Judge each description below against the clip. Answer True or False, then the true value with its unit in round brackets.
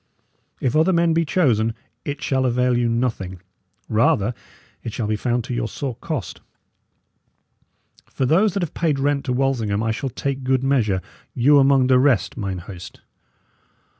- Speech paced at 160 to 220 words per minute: True (165 wpm)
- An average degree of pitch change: True (3.8 semitones)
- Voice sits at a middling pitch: False (125 Hz)